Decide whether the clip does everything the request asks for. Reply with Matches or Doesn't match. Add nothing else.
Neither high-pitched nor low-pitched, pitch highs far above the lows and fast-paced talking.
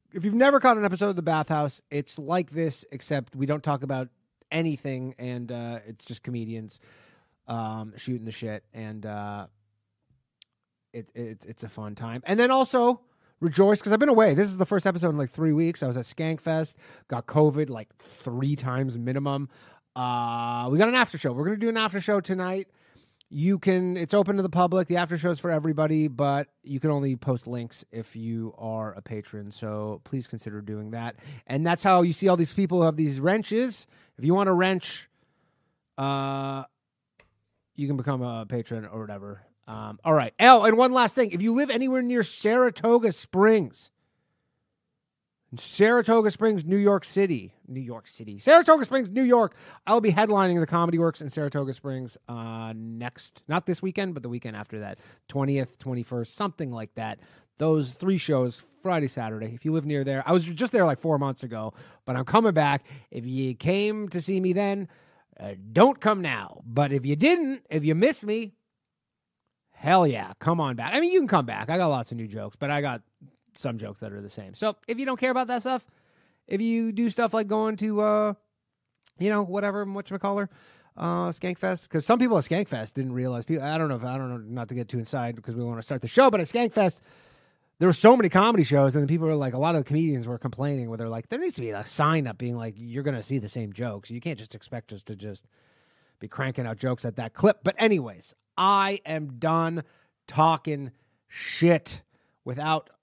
Matches